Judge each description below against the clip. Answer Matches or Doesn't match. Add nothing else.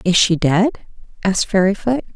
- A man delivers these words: Doesn't match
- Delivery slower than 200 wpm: Matches